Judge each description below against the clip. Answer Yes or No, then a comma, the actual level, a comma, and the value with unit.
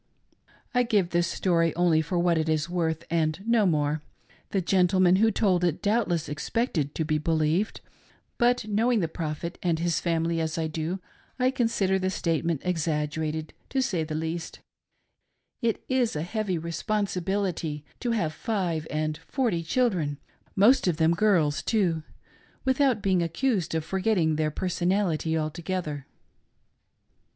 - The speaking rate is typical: Yes, average, 150 wpm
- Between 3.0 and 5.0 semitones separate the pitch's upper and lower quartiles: Yes, average, 4.2 semitones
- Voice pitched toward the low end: No, medium, 170 Hz